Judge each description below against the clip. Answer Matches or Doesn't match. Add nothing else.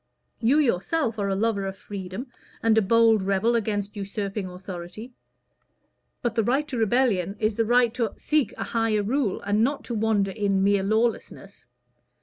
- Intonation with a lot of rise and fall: Doesn't match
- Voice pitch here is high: Matches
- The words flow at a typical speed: Matches